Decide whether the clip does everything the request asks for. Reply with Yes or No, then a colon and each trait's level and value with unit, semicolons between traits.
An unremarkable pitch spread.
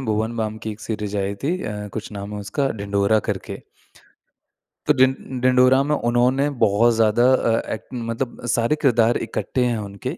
Yes: average, 3.4 semitones